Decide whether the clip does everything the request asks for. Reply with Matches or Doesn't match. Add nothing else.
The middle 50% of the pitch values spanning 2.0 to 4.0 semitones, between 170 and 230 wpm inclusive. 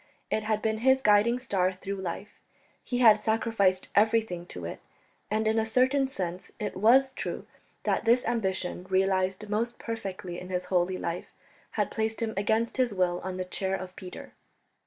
Matches